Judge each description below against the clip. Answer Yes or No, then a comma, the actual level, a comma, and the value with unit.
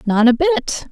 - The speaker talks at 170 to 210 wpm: Yes, average, 200 wpm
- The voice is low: No, very high, 260 Hz